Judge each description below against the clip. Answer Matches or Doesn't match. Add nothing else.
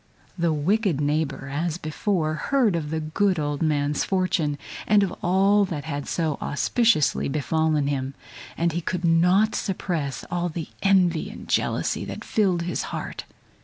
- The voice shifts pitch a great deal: Doesn't match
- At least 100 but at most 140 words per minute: Doesn't match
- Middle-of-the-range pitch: Matches